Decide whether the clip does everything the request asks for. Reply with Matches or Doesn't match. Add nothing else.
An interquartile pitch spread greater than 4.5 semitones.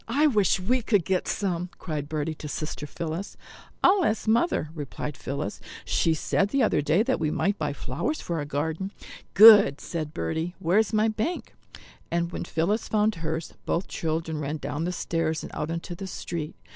Matches